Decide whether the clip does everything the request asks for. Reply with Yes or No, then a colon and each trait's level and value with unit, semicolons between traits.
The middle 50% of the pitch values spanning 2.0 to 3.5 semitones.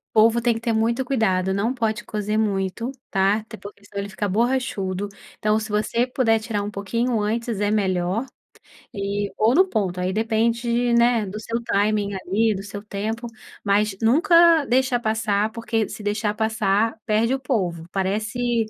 Yes: narrow, 2.5 semitones